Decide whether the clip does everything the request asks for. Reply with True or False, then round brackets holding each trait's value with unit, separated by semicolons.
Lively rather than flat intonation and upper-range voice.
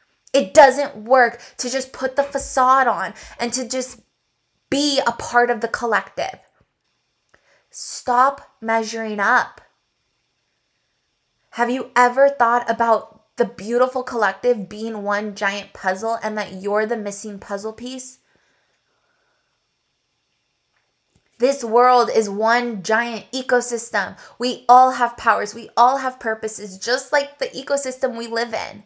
False (2.7 semitones; 240 Hz)